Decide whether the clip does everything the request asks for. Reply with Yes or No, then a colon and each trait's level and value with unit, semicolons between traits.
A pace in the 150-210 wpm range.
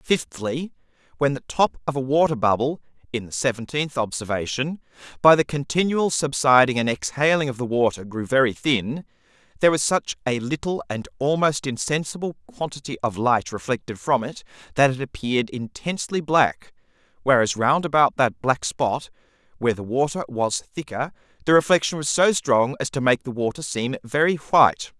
Yes: average, 160 wpm